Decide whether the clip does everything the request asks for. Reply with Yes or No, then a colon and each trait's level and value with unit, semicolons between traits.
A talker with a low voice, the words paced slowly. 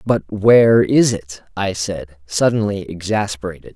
Yes: very low, 95 Hz; slow, 130 wpm